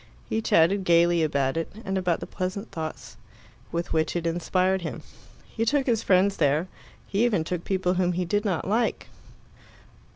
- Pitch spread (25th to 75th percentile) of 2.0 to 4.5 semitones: Yes, average, 3.1 semitones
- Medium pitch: Yes, medium, 180 Hz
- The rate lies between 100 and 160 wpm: No, average, 170 wpm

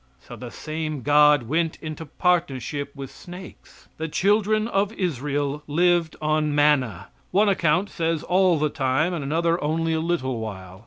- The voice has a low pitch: No, medium, 155 Hz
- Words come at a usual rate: Yes, average, 155 wpm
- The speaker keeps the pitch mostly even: No, average, 3.3 semitones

